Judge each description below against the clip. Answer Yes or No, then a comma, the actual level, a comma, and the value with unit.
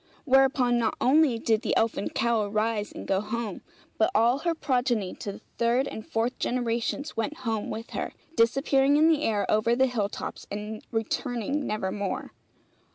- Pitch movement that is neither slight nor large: Yes, average, 3.5 semitones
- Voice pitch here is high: Yes, high, 230 Hz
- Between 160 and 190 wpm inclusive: Yes, average, 165 wpm